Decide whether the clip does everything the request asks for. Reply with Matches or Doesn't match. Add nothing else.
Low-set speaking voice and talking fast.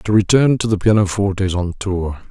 Matches